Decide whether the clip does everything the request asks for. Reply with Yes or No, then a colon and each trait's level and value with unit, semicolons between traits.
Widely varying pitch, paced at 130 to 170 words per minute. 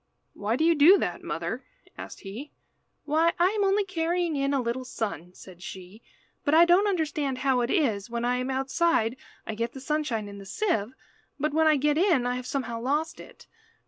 No: wide, 5.7 semitones; fast, 205 wpm